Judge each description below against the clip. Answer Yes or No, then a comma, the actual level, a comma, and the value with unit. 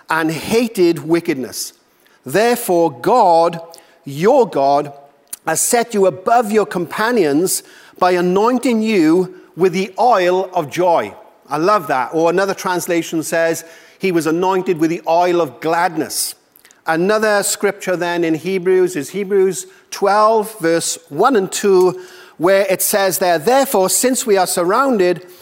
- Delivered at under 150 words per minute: Yes, slow, 135 wpm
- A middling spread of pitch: Yes, average, 3.2 semitones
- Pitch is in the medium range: Yes, medium, 180 Hz